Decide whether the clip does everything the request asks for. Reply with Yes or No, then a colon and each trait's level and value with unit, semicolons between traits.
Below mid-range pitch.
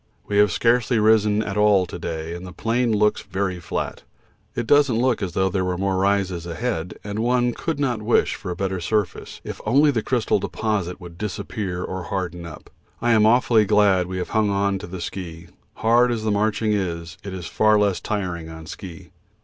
Yes: low, 100 Hz